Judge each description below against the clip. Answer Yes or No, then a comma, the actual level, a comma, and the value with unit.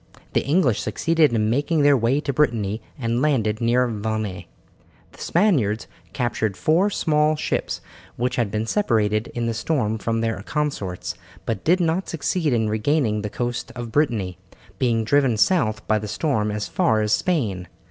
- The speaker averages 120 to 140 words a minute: No, average, 165 wpm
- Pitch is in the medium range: No, low, 115 Hz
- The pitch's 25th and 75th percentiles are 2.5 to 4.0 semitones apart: No, wide, 5.5 semitones